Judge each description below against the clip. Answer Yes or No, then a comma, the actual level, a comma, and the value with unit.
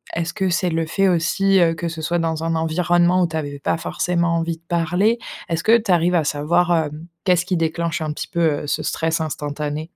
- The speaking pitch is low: No, medium, 165 Hz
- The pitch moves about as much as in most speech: No, narrow, 1.7 semitones